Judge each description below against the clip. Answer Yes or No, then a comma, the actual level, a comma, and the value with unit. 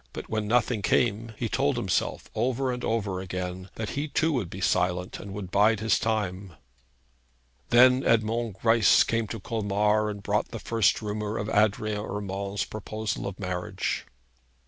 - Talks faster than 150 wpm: Yes, average, 165 wpm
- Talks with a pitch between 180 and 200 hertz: No, low, 105 Hz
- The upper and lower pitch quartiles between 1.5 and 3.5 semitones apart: Yes, narrow, 2.5 semitones